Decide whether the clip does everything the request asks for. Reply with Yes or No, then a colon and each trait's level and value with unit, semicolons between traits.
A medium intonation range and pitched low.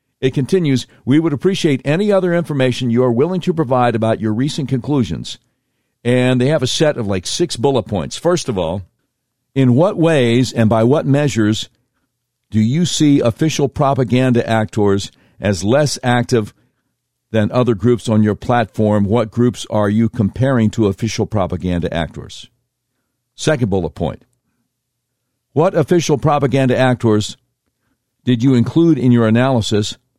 Yes: average, 3.5 semitones; low, 125 Hz